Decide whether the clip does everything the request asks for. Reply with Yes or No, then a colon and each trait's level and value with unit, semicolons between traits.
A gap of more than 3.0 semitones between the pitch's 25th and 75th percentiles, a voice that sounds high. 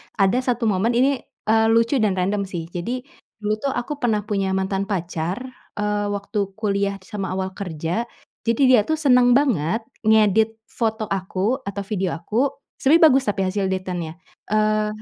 Yes: average, 3.4 semitones; high, 210 Hz